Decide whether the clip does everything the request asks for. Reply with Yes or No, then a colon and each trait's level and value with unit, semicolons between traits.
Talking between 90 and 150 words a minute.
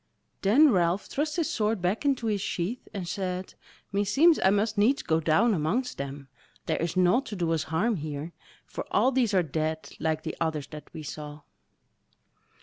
No: average, 180 wpm